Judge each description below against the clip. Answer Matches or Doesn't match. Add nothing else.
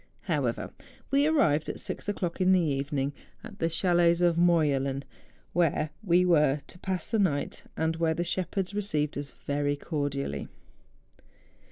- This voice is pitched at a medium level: Matches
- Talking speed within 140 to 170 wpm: Matches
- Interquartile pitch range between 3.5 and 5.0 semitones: Matches